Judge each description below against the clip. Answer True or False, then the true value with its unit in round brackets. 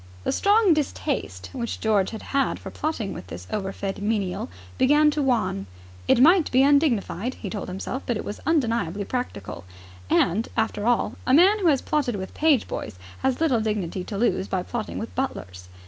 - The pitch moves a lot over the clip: True (6.4 semitones)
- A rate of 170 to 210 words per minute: True (180 wpm)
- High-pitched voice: True (230 Hz)